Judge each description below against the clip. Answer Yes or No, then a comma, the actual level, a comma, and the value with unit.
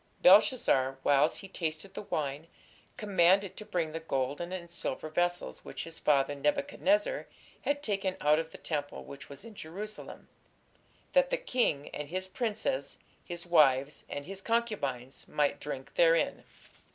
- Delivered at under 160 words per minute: Yes, average, 150 wpm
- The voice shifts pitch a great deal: Yes, wide, 6.2 semitones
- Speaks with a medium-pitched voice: Yes, medium, 170 Hz